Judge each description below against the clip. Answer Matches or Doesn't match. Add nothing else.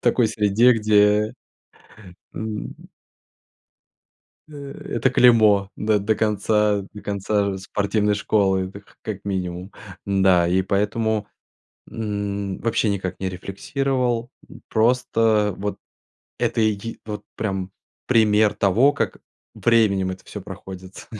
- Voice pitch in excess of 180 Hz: Doesn't match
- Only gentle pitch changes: Matches